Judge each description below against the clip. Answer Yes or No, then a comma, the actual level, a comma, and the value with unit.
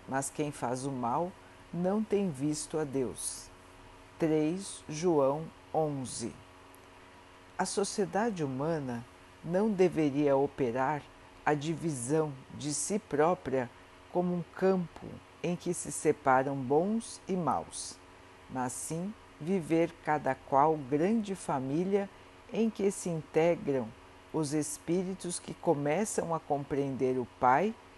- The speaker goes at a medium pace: No, slow, 115 wpm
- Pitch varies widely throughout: Yes, wide, 6.0 semitones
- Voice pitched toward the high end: No, medium, 150 Hz